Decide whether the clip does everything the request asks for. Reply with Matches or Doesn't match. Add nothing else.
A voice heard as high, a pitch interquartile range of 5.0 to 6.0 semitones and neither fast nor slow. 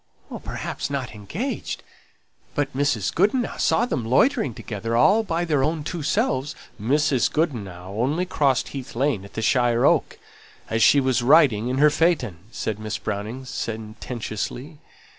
Doesn't match